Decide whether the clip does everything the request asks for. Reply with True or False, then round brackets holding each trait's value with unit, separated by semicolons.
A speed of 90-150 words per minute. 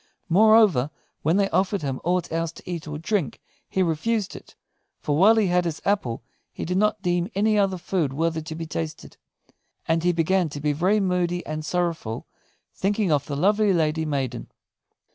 False (180 wpm)